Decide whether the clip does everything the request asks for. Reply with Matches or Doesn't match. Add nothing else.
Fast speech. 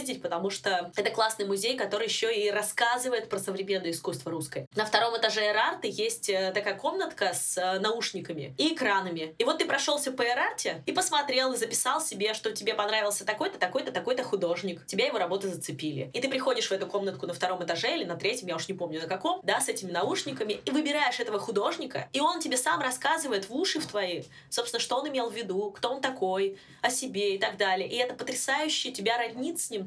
Matches